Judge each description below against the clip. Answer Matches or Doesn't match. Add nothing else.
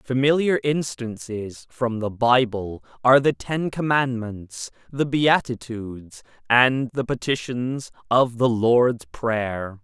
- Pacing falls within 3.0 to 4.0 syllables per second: Matches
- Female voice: Doesn't match